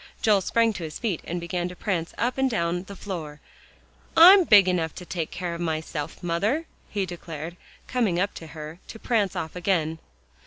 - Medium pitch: Yes, medium, 180 Hz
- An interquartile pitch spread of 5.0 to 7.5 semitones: No, average, 3.9 semitones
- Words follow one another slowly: No, average, 190 wpm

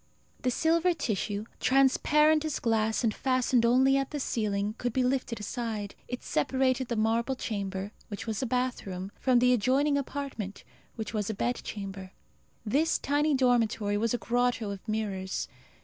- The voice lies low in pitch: No, high, 240 Hz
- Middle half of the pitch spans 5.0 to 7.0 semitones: No, average, 4.0 semitones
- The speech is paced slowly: No, average, 160 wpm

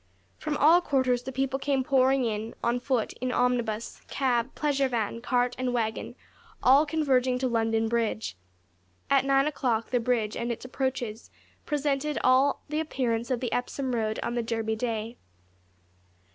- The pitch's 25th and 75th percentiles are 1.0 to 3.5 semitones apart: Yes, average, 2.8 semitones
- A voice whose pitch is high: Yes, very high, 250 Hz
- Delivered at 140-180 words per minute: Yes, average, 160 wpm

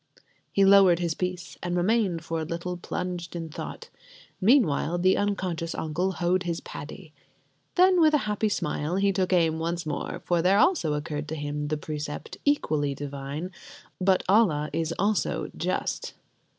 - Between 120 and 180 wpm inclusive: Yes, average, 160 wpm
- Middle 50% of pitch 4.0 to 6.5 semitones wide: No, average, 3.6 semitones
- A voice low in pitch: No, medium, 175 Hz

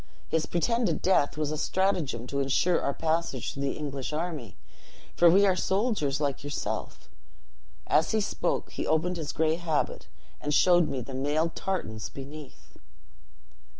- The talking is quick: No, average, 150 wpm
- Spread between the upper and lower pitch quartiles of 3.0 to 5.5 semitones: Yes, average, 4.1 semitones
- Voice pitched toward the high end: No, medium, 155 Hz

